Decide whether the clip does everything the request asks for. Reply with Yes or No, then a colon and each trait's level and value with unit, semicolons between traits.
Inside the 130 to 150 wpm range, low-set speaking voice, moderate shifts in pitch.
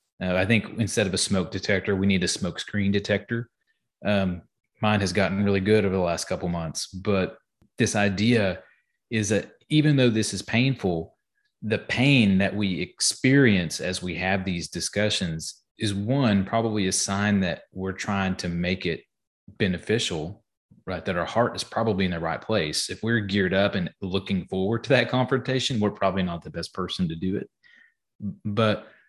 No: average, 180 wpm; low, 100 Hz; average, 3.2 semitones